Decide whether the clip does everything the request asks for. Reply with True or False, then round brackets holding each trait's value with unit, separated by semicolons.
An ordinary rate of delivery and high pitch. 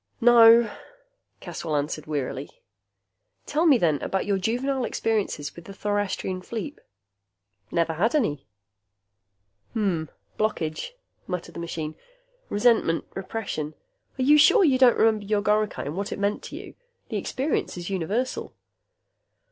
False (130 wpm; 205 Hz)